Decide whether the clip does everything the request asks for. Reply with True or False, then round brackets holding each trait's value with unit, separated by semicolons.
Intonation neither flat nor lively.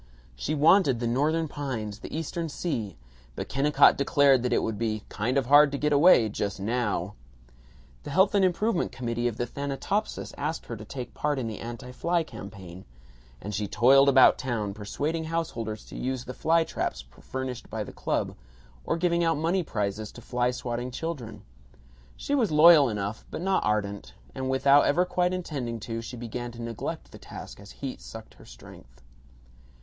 False (5.7 semitones)